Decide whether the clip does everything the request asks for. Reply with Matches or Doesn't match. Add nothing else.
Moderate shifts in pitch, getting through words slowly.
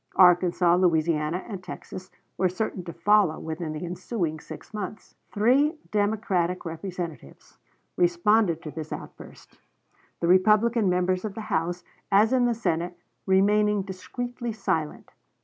Matches